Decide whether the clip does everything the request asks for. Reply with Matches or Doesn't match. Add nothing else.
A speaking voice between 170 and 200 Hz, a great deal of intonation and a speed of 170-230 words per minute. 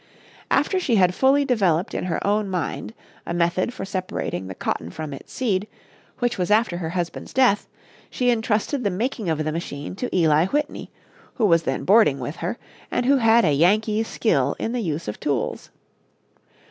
Matches